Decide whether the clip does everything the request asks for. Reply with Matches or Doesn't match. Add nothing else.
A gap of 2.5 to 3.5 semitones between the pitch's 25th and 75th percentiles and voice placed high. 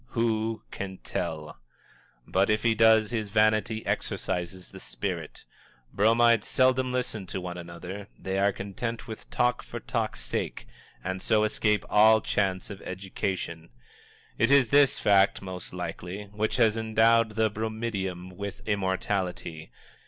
Doesn't match